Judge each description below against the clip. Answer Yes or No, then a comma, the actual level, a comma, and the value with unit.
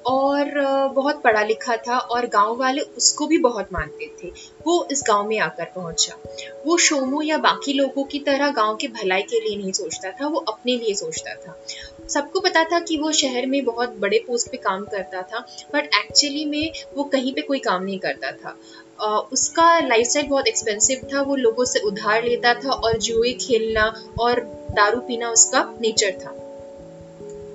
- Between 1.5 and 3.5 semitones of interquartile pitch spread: No, average, 5.3 semitones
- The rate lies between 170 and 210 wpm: Yes, average, 185 wpm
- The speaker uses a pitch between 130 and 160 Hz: No, high, 245 Hz